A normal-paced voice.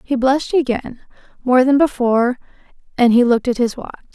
Yes: average, 175 wpm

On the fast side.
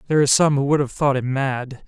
Yes: fast, 290 wpm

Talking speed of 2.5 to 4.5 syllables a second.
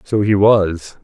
Yes: 3.3 syllables/s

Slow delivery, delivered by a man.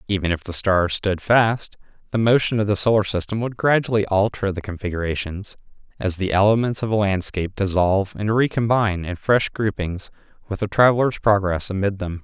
No: average, 170 wpm; male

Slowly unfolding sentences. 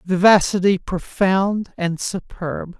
Yes: slow, 85 wpm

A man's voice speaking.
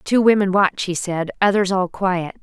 No: female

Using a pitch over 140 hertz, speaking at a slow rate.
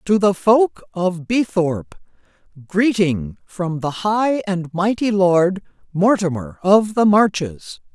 Yes: high, 190 Hz; slow, 115 wpm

